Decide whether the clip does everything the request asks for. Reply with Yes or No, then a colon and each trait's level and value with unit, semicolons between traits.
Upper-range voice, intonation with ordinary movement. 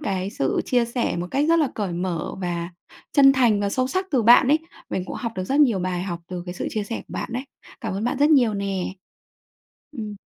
No: high, 215 Hz; wide, 6.0 semitones